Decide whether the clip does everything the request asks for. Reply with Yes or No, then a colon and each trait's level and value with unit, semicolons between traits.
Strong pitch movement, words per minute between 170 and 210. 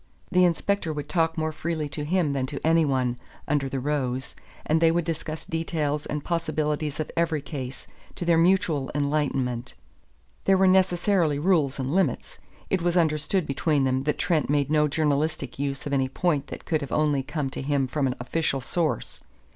No: average, 3.0 semitones; average, 185 wpm